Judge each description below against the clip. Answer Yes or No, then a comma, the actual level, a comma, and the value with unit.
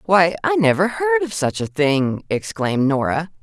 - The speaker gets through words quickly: No, average, 175 wpm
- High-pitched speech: No, medium, 175 Hz